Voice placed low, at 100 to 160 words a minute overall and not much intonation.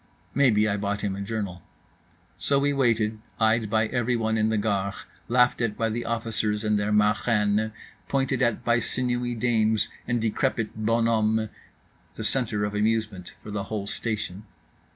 Yes: low, 110 Hz; average, 150 wpm; narrow, 1.9 semitones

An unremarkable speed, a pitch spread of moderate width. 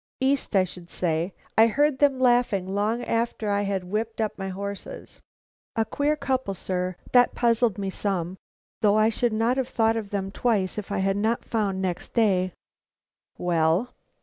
Yes: average, 175 wpm; average, 3.7 semitones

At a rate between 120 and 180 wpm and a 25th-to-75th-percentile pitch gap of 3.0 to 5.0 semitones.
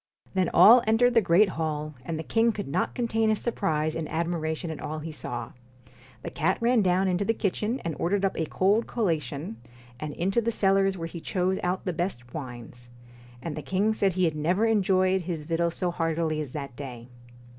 No: average, 200 wpm; average, 4.2 semitones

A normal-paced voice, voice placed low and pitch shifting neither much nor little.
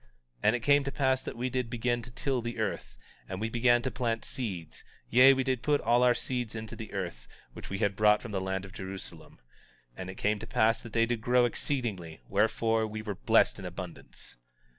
No: fast, 225 wpm; low, 115 Hz; average, 3.0 semitones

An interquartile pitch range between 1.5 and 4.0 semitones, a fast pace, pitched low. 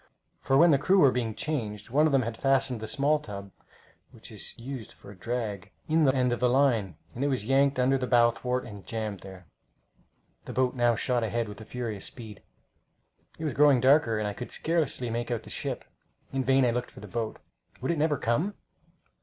Yes: average, 3.4 semitones; fast, 215 wpm; low, 125 Hz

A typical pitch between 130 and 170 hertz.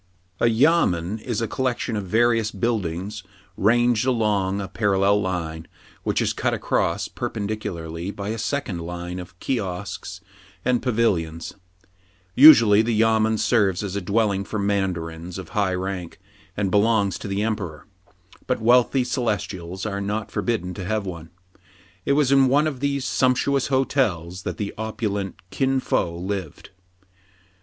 No: low, 105 Hz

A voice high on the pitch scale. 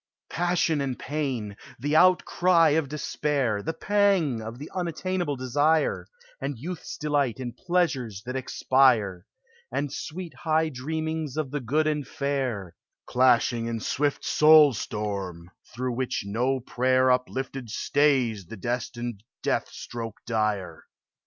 No: low, 130 Hz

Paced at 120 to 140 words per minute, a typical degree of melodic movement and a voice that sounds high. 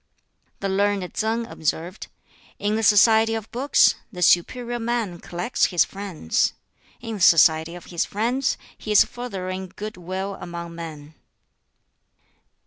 Yes: slow, 135 wpm; average, 4.4 semitones; high, 195 Hz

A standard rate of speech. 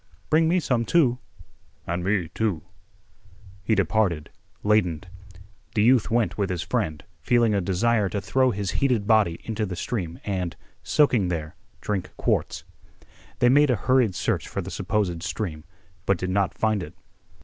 Yes: average, 160 wpm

